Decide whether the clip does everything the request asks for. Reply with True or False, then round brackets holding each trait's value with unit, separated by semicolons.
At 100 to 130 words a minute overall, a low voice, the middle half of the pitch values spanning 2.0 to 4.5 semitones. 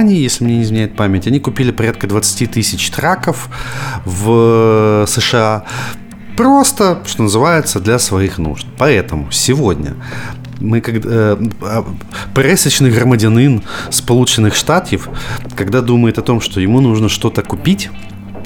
True (125 wpm; 115 Hz; 3.4 semitones)